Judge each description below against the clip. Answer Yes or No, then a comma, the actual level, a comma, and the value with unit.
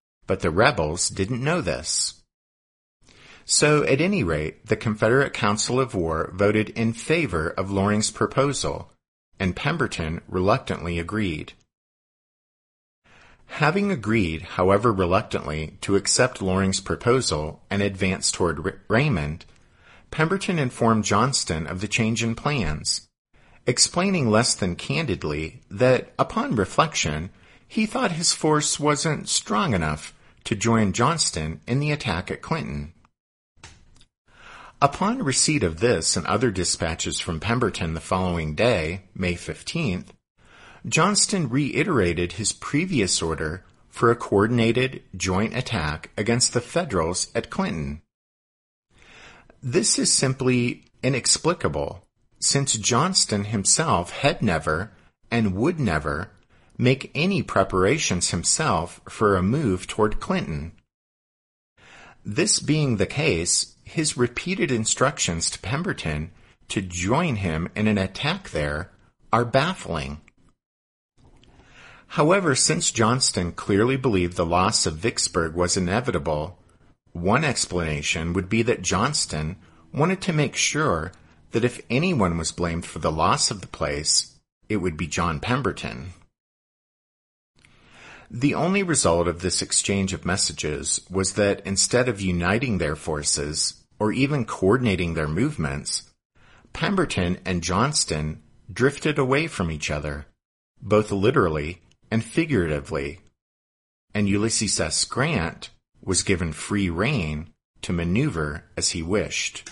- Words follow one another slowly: Yes, slow, 120 wpm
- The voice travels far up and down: Yes, wide, 6.6 semitones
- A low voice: Yes, low, 100 Hz